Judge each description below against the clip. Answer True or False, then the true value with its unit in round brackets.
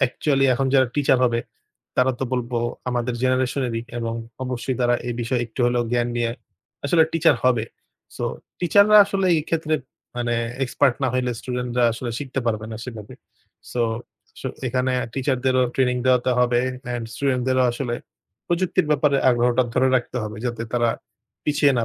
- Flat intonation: True (2.1 semitones)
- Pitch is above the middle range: False (125 Hz)